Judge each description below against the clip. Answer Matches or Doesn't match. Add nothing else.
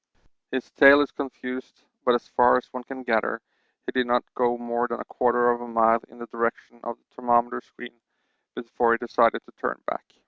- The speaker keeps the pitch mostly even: Matches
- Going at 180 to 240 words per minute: Matches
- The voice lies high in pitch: Doesn't match